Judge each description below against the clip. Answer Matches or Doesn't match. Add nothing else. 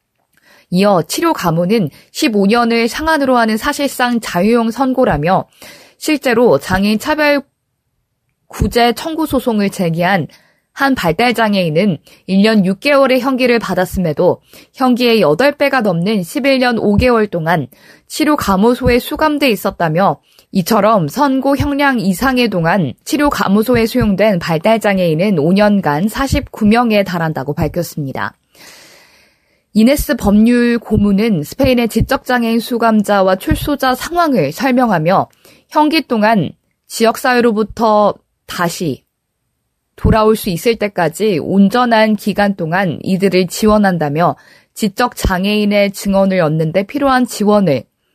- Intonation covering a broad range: Doesn't match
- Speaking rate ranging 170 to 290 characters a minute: Matches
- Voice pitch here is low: Doesn't match